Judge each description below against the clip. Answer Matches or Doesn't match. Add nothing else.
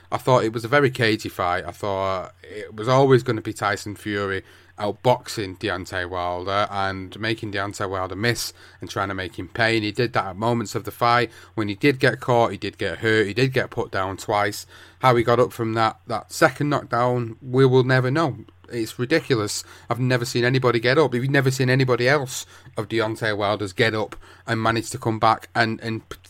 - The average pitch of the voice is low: Matches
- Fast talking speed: Matches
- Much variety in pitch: Doesn't match